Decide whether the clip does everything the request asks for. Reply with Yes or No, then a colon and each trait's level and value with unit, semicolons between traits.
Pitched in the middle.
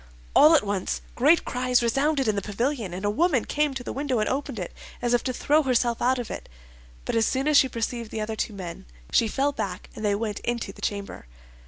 No: high, 240 Hz